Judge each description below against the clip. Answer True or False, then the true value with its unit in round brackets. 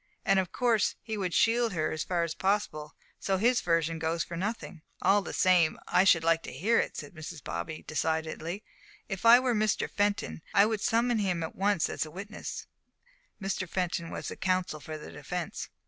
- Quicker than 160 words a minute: True (195 wpm)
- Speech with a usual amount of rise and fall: True (4.2 semitones)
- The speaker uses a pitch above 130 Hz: True (185 Hz)